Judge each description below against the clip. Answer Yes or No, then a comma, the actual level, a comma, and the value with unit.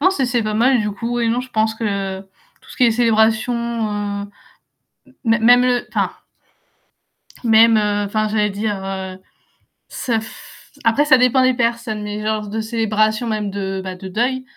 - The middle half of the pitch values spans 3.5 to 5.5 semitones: No, narrow, 2.6 semitones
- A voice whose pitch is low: No, high, 220 Hz